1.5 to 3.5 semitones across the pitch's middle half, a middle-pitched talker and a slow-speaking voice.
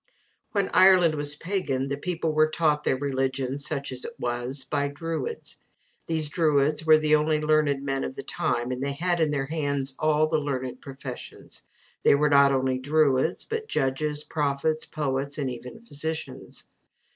No: narrow, 2.5 semitones; medium, 145 Hz; average, 170 wpm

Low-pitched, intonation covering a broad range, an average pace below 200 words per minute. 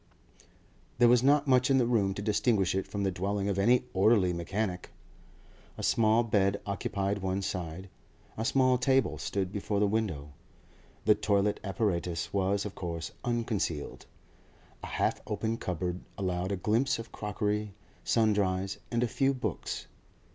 No: low, 100 Hz; average, 3.3 semitones; average, 150 wpm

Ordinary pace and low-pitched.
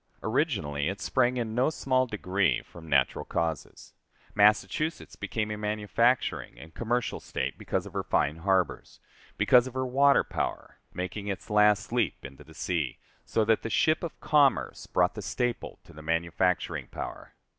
Yes: average, 160 wpm; low, 105 Hz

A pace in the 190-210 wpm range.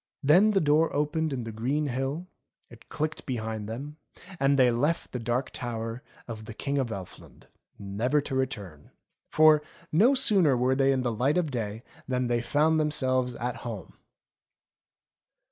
No: average, 160 wpm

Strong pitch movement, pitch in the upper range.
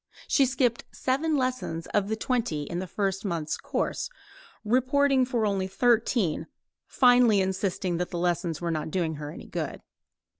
Yes: wide, 6.4 semitones; high, 200 Hz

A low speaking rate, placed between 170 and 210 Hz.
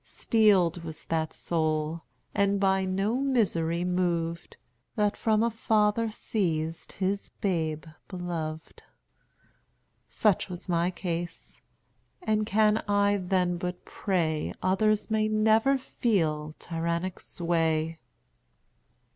Yes: slow, 105 wpm; medium, 185 Hz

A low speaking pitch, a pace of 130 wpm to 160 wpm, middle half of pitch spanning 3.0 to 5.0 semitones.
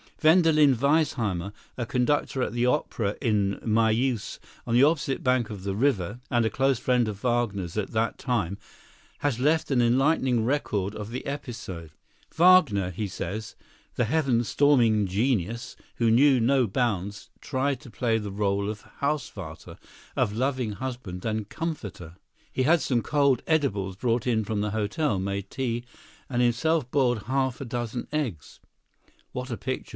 Yes: low, 120 Hz; average, 155 wpm; average, 4.4 semitones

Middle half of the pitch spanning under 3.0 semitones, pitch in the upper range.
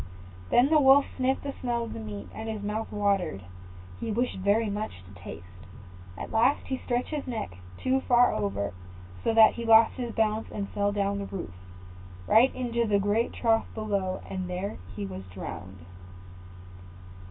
No: average, 4.2 semitones; high, 215 Hz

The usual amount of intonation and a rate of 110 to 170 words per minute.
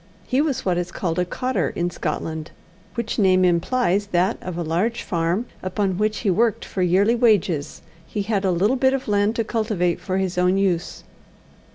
No: average, 4.0 semitones; average, 190 wpm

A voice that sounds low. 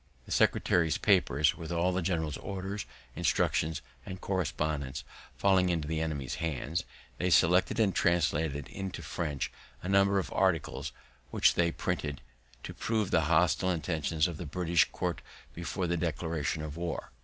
Yes: very low, 85 Hz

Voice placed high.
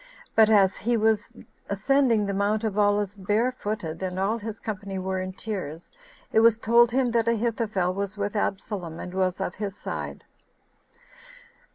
Yes: high, 205 Hz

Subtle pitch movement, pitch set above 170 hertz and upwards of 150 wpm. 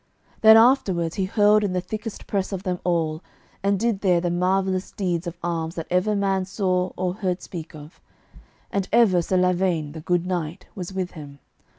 Yes: narrow, 2.1 semitones; medium, 185 Hz; average, 190 wpm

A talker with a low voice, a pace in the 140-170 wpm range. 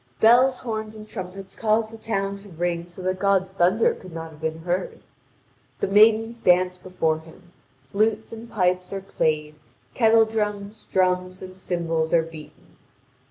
No: high, 190 Hz; average, 160 wpm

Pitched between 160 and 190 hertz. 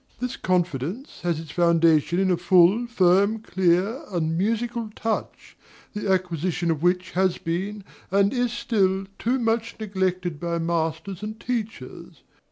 Yes: medium, 185 Hz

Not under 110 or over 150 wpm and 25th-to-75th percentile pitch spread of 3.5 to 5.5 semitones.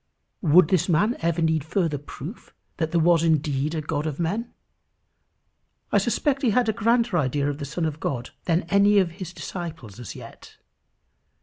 No: average, 180 wpm; average, 4.6 semitones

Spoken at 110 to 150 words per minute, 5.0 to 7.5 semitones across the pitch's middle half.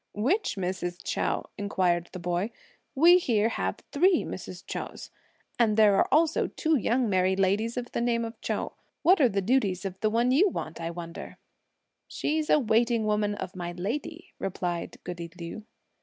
No: average, 175 wpm; wide, 5.5 semitones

